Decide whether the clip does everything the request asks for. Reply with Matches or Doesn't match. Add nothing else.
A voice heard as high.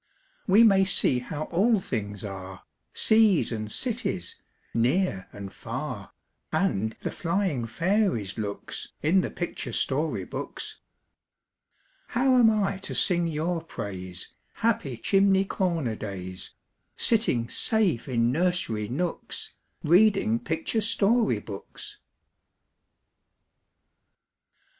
Doesn't match